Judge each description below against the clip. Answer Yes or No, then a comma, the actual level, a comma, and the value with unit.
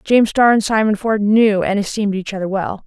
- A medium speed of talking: No, fast, 230 wpm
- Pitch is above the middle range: Yes, high, 205 Hz